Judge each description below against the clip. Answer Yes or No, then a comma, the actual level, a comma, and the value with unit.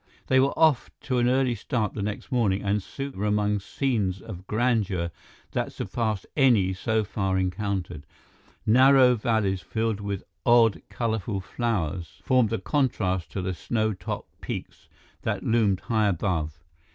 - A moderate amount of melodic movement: Yes, average, 4.0 semitones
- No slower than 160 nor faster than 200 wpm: No, average, 150 wpm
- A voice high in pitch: No, low, 105 Hz